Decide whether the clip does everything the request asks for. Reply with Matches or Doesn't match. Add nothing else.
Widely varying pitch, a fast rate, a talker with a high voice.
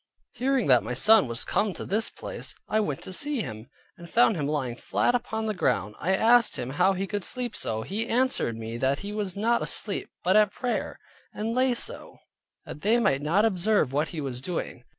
Matches